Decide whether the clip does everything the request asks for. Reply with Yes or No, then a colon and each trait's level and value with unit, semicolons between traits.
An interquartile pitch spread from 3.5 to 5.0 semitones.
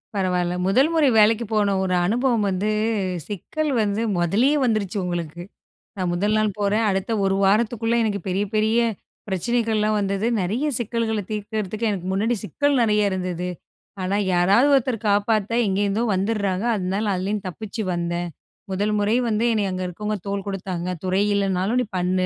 No: average, 2.9 semitones